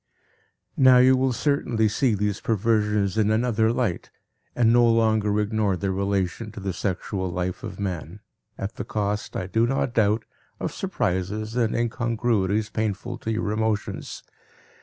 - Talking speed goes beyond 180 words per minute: No, average, 150 wpm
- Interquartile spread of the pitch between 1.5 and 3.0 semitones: Yes, narrow, 2.5 semitones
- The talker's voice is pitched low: Yes, low, 110 Hz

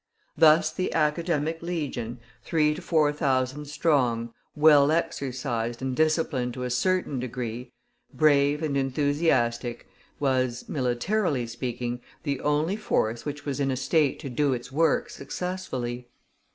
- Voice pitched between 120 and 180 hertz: Yes, medium, 140 Hz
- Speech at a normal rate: No, slow, 130 wpm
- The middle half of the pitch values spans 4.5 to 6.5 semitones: No, average, 3.9 semitones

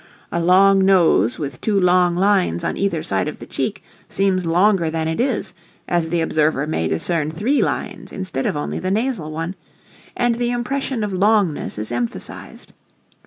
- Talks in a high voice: No, medium, 180 Hz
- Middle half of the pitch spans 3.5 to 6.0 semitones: Yes, average, 4.3 semitones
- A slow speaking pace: No, average, 170 wpm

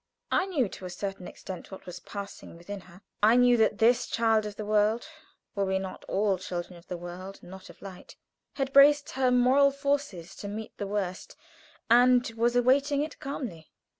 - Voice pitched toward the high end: Yes, high, 210 Hz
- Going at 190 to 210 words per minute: Yes, average, 195 wpm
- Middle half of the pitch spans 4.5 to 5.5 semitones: Yes, average, 4.8 semitones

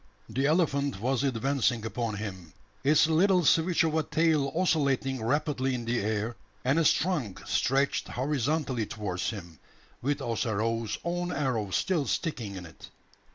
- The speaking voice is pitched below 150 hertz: Yes, low, 135 Hz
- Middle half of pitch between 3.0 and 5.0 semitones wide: No, wide, 5.6 semitones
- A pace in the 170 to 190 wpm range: No, average, 145 wpm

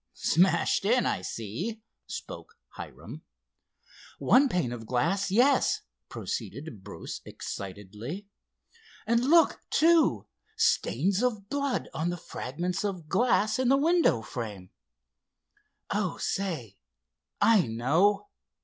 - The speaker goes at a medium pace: No, slow, 105 wpm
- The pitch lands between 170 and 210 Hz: Yes, high, 190 Hz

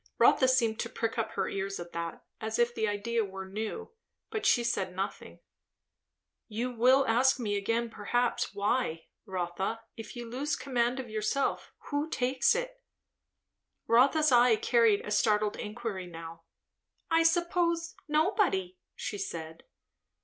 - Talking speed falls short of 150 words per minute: Yes, average, 140 wpm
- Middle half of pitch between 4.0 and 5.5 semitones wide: Yes, average, 4.4 semitones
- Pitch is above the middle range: Yes, high, 230 Hz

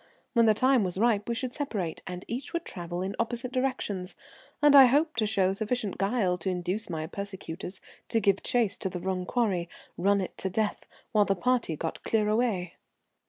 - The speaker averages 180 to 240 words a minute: Yes, average, 200 wpm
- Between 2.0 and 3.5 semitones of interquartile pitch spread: No, average, 4.7 semitones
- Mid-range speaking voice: No, high, 205 Hz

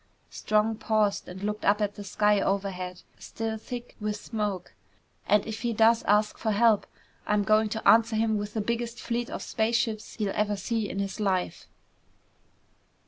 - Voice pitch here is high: Yes, high, 215 Hz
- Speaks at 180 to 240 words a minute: No, average, 170 wpm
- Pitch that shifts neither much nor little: No, narrow, 1.6 semitones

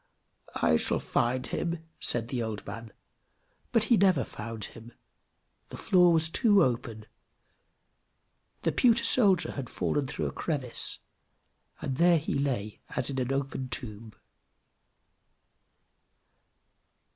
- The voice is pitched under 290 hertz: Yes, low, 135 Hz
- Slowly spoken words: Yes, slow, 120 wpm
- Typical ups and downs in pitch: No, wide, 7.0 semitones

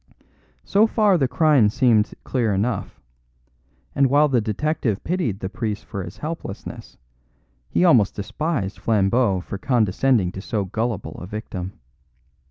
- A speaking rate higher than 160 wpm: No, slow, 135 wpm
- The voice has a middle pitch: No, low, 115 Hz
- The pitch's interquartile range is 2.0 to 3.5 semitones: No, wide, 5.6 semitones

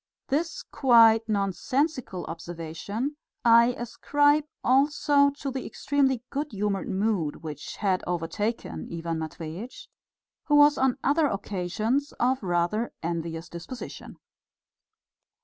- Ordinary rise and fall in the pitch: No, wide, 7.8 semitones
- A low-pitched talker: No, high, 225 Hz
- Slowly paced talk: Yes, slow, 105 wpm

